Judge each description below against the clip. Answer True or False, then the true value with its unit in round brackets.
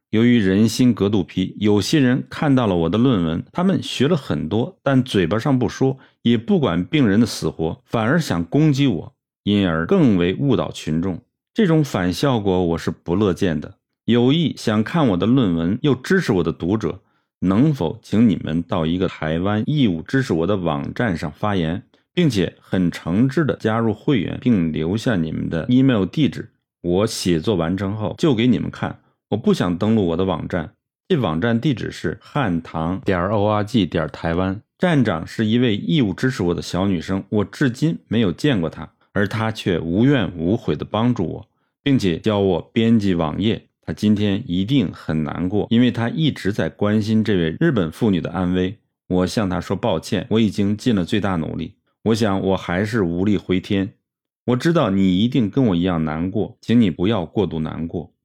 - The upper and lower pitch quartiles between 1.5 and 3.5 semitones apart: False (5.2 semitones)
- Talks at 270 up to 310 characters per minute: True (275 characters per minute)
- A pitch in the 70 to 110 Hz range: True (105 Hz)